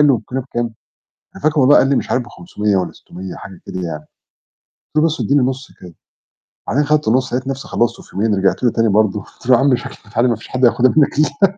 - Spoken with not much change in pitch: No, average, 4.3 semitones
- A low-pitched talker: Yes, low, 125 Hz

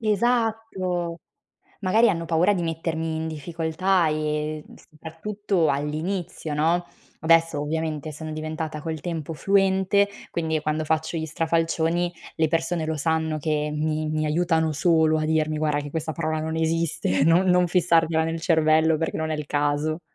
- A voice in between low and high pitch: Yes, medium, 160 Hz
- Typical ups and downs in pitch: No, narrow, 1.7 semitones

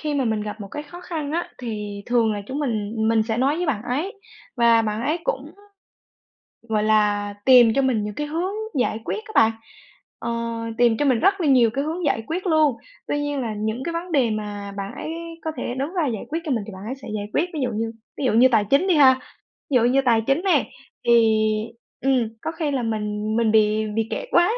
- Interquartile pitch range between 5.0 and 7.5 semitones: Yes, average, 5.3 semitones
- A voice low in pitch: No, high, 245 Hz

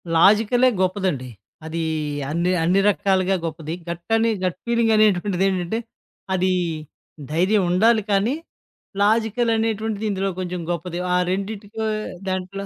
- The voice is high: Yes, high, 195 Hz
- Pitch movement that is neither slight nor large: Yes, average, 3.4 semitones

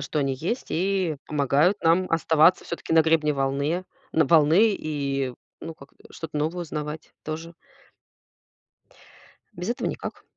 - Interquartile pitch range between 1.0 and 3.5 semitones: Yes, average, 2.7 semitones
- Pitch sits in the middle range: Yes, medium, 160 Hz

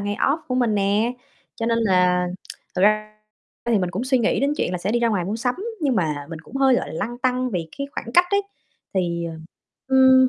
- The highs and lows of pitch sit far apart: Yes, wide, 5.8 semitones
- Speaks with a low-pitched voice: No, high, 220 Hz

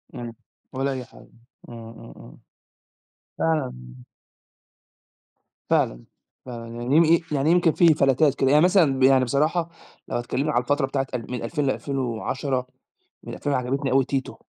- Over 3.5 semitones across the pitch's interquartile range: No, average, 3.0 semitones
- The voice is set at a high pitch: No, low, 135 Hz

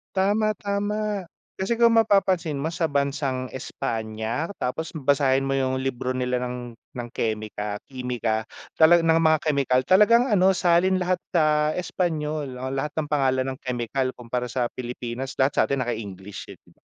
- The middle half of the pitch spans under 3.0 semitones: No, average, 5.2 semitones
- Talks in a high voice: No, low, 135 Hz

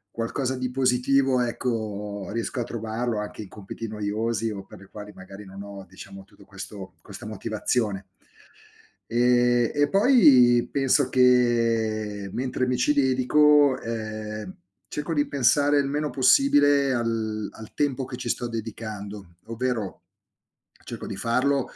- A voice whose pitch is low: Yes, low, 120 Hz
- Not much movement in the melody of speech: No, average, 3.6 semitones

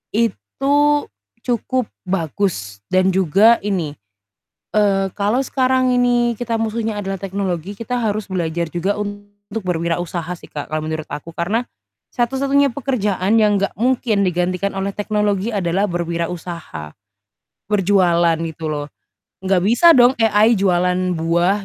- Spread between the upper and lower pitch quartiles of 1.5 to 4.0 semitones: No, average, 4.4 semitones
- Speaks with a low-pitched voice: No, high, 195 Hz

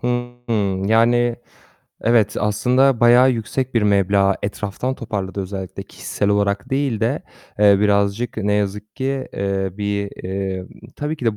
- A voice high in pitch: No, low, 105 Hz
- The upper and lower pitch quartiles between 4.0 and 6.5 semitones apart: No, average, 3.3 semitones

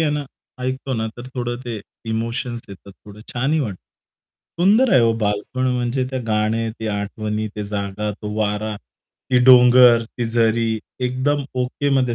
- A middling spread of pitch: Yes, average, 3.1 semitones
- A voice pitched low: Yes, low, 120 Hz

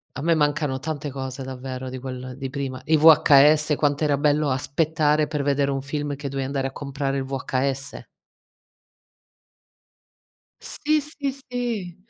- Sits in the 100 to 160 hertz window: Yes, medium, 140 Hz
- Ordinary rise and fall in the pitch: No, narrow, 2.3 semitones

